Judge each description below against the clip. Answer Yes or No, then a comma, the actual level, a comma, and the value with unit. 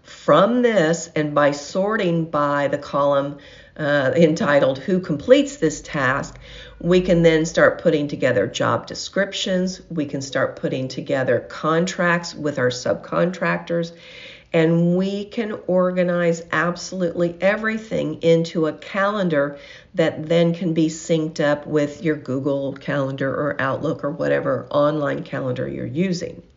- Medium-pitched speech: Yes, medium, 165 Hz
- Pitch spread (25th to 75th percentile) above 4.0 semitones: No, average, 3.5 semitones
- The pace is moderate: No, slow, 130 wpm